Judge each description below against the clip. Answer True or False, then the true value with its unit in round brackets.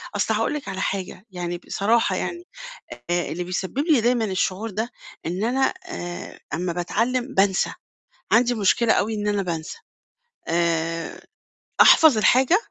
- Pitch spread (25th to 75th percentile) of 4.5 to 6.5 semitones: True (5.2 semitones)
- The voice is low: False (205 Hz)